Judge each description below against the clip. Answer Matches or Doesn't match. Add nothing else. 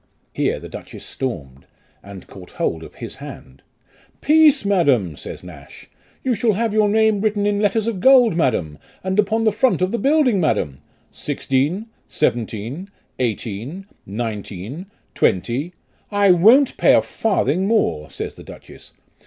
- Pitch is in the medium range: Matches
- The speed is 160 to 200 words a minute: Doesn't match